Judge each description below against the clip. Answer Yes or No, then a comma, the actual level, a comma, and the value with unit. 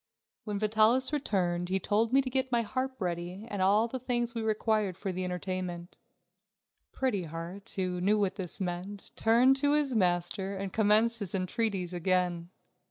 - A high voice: Yes, high, 200 Hz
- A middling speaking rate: Yes, average, 165 wpm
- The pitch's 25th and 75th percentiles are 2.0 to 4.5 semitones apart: Yes, average, 4.1 semitones